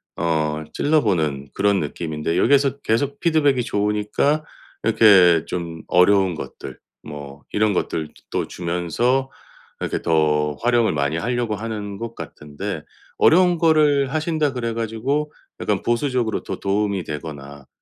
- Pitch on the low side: Yes, low, 105 Hz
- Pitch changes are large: Yes, wide, 8.4 semitones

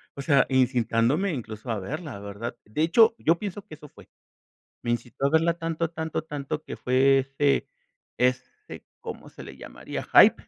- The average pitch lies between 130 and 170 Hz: Yes, medium, 140 Hz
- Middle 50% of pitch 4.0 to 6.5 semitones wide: Yes, average, 4.9 semitones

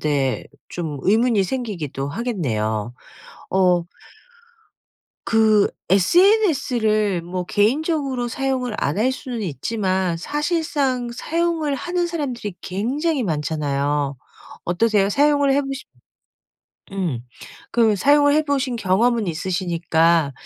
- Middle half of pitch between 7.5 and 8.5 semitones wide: Yes, wide, 7.8 semitones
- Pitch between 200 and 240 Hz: Yes, high, 215 Hz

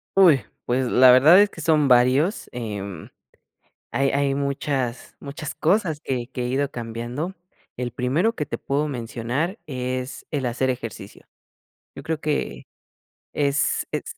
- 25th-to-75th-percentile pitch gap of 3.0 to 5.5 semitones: Yes, average, 3.5 semitones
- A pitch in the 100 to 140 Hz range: Yes, low, 135 Hz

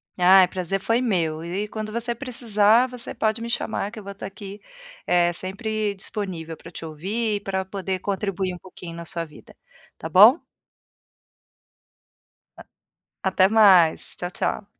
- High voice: Yes, high, 195 Hz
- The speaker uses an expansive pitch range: No, average, 3.3 semitones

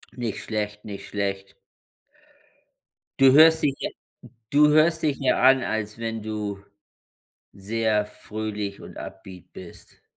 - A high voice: No, low, 110 Hz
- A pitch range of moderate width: Yes, average, 4.5 semitones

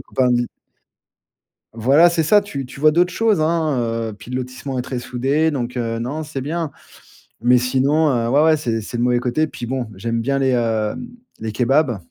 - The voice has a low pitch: Yes, low, 130 Hz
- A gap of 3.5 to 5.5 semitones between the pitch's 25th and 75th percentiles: Yes, average, 4.3 semitones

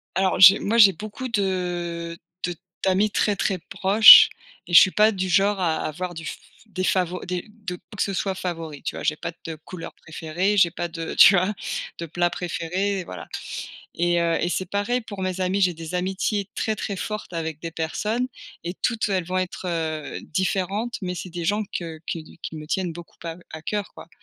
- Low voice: No, medium, 180 Hz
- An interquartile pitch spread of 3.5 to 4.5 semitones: No, average, 3.0 semitones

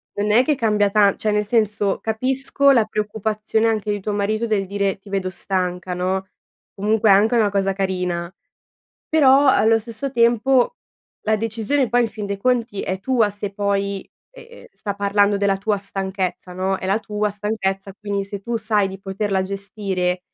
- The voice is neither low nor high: No, high, 205 Hz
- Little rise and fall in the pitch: Yes, narrow, 2.2 semitones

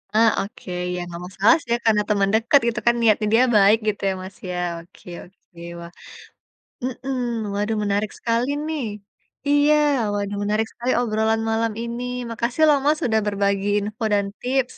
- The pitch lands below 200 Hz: No, high, 220 Hz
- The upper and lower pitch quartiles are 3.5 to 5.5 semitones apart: No, average, 2.7 semitones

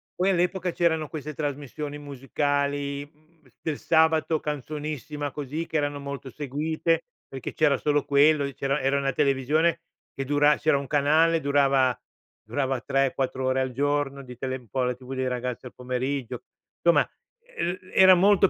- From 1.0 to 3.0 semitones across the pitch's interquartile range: Yes, narrow, 2.5 semitones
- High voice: No, medium, 145 Hz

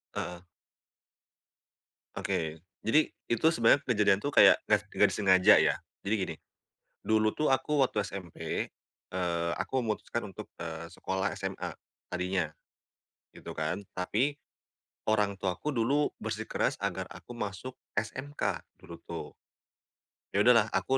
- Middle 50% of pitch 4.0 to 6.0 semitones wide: Yes, average, 5.0 semitones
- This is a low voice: Yes, low, 100 Hz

